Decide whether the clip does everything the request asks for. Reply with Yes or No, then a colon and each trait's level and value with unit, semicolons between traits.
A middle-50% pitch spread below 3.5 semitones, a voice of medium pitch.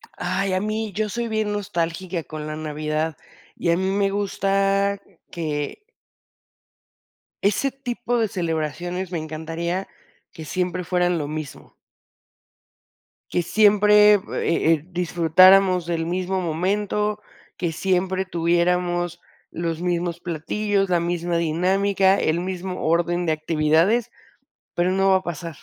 Yes: average, 2.9 semitones; medium, 180 Hz